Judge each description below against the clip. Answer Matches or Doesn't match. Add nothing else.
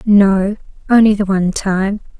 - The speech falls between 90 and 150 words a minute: Matches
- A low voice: Doesn't match